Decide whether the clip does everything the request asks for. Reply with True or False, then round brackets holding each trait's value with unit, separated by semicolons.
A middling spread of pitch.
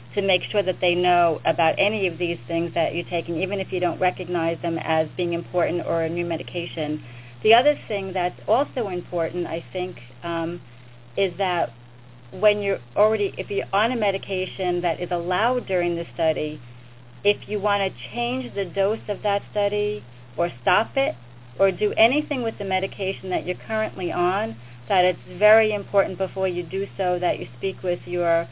True (3.1 semitones)